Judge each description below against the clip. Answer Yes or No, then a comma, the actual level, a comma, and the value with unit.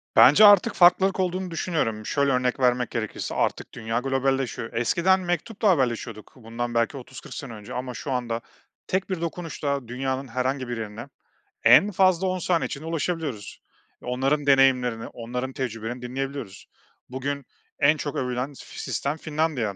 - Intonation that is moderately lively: Yes, average, 4.8 semitones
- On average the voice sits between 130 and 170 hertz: Yes, low, 135 Hz